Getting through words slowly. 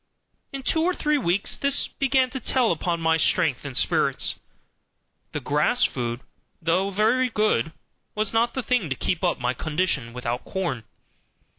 No: average, 160 wpm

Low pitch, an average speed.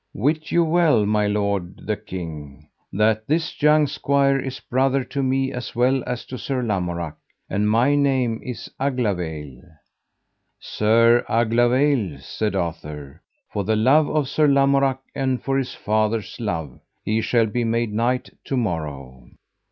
Yes: low, 115 Hz; average, 145 wpm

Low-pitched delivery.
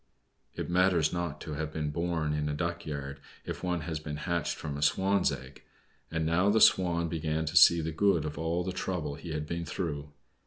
Yes: very low, 80 Hz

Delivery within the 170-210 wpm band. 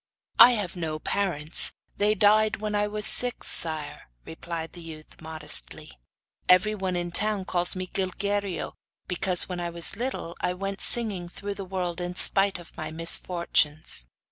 No: average, 160 wpm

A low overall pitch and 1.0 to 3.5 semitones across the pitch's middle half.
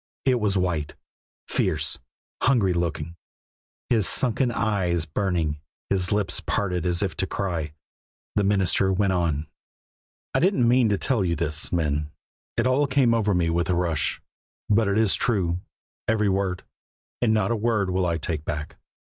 No: very low, 95 Hz; average, 4.2 semitones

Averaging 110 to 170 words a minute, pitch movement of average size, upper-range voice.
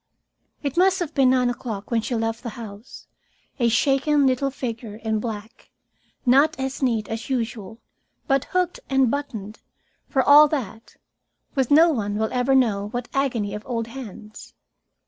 Yes: average, 160 wpm; average, 3.6 semitones; high, 245 Hz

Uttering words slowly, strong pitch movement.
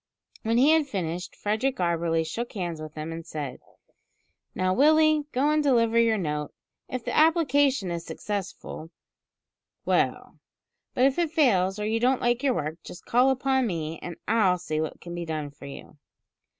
No: average, 175 wpm; wide, 8.0 semitones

